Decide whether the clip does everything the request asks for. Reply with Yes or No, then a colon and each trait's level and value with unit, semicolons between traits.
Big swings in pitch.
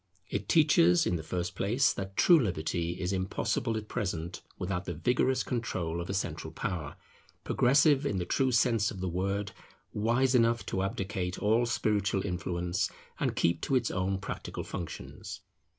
No: average, 4.7 semitones